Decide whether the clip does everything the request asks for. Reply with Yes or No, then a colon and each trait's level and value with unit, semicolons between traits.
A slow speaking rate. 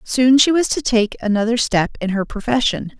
No: average, 200 wpm